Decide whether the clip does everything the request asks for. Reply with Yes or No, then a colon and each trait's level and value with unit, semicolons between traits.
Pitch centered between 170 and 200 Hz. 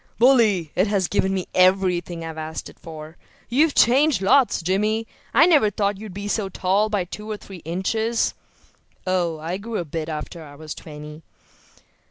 Yes: high, 190 Hz